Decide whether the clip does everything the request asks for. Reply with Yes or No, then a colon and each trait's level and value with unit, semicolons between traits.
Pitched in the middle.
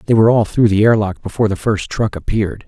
No: low, 105 Hz